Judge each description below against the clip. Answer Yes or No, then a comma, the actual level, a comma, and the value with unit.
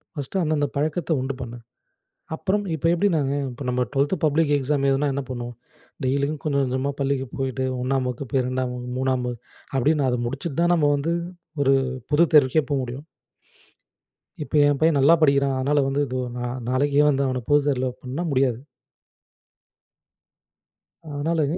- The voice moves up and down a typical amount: No, narrow, 2.3 semitones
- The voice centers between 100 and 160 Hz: Yes, medium, 140 Hz